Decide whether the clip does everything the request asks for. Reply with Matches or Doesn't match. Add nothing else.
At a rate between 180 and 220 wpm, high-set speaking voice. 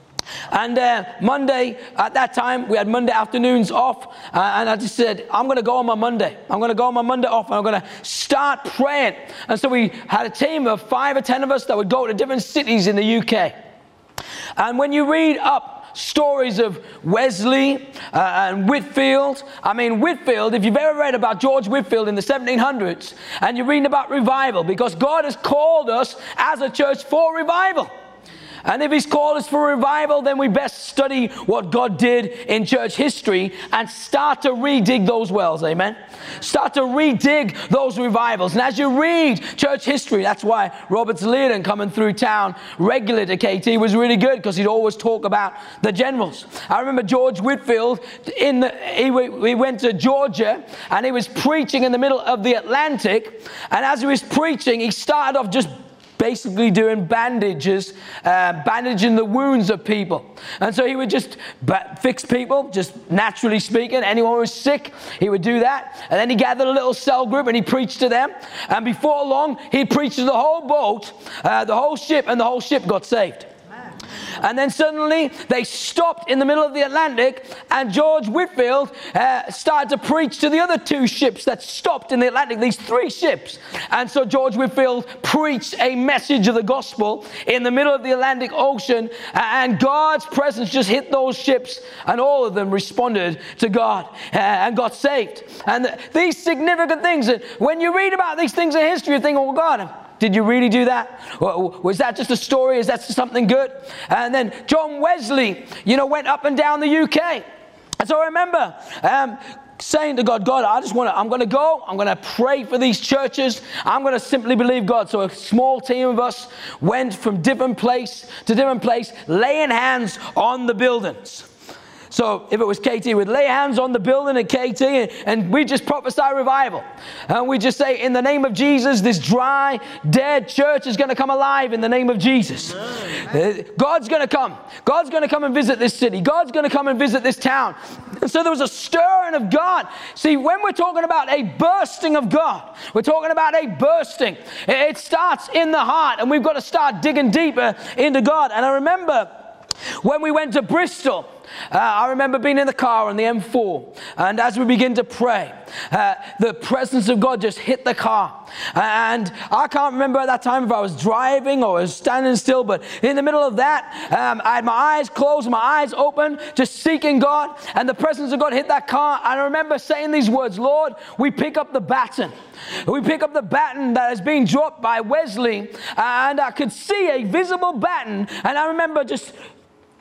Matches